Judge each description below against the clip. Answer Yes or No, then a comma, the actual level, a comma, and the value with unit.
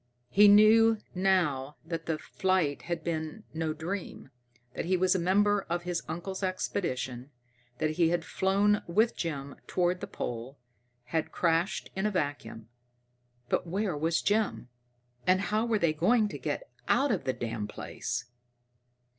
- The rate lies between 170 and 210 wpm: No, average, 155 wpm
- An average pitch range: Yes, average, 4.4 semitones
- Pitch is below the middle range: No, medium, 175 Hz